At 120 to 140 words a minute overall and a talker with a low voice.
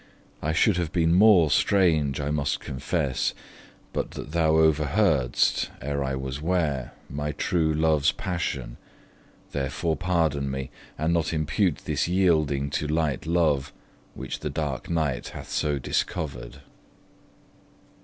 Yes: slow, 135 wpm; very low, 75 Hz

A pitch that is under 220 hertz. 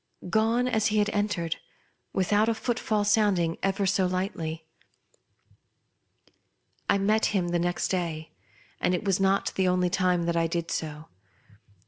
Yes: high, 190 Hz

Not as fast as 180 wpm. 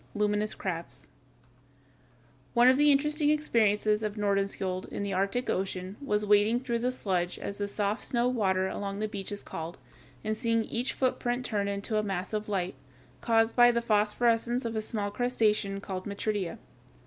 Yes: average, 170 wpm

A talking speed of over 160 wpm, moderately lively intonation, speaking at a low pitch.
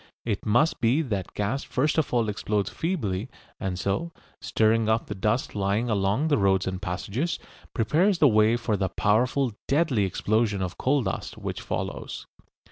Yes: average, 170 wpm; average, 4.9 semitones; low, 110 Hz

